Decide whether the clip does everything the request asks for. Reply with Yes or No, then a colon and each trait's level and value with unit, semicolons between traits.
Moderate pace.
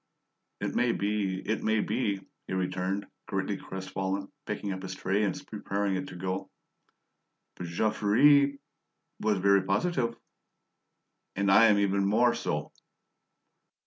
No: slow, 130 wpm